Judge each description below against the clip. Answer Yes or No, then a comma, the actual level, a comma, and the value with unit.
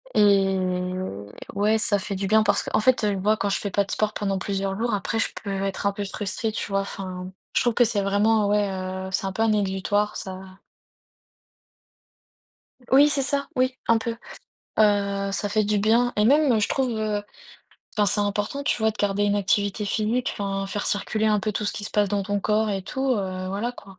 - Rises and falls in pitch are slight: Yes, narrow, 1.8 semitones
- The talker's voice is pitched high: Yes, high, 205 Hz